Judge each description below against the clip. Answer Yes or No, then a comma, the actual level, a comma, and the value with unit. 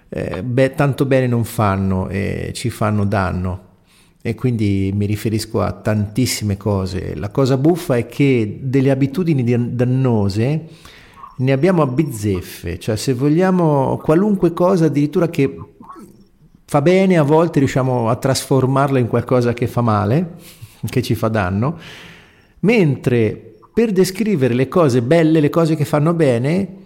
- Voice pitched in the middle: No, low, 130 Hz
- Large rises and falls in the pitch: Yes, wide, 6.3 semitones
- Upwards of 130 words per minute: Yes, average, 145 wpm